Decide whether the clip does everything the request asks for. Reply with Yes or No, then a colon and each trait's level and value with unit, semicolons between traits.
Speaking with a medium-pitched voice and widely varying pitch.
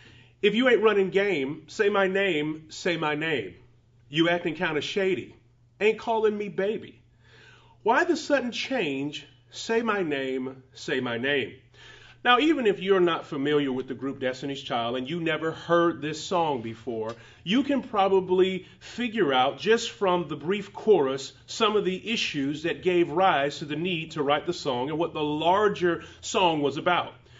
Yes: medium, 170 Hz; wide, 6.3 semitones